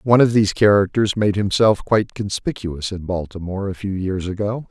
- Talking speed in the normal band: Yes, average, 180 wpm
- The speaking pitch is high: No, low, 100 Hz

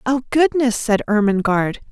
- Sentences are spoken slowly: Yes, slow, 125 wpm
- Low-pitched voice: No, high, 230 Hz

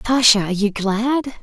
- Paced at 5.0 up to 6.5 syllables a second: Yes, 6.0 syllables/s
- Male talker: No, female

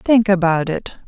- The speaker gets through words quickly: No, average, 165 wpm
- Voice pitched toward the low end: No, high, 190 Hz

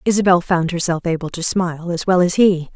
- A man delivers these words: No, female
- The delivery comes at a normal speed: No, fast, 220 wpm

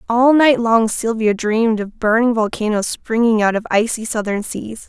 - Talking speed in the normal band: Yes, average, 170 wpm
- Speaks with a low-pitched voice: No, high, 225 Hz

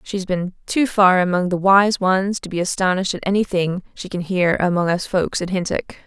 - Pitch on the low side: No, medium, 185 Hz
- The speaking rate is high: Yes, fast, 210 wpm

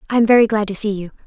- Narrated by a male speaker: No, female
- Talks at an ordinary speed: No, fast, 285 wpm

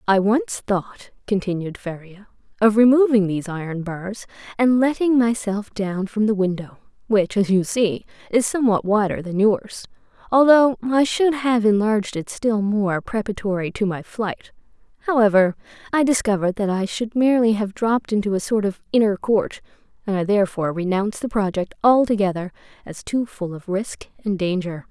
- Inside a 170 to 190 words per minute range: No, average, 160 wpm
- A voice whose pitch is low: No, high, 210 Hz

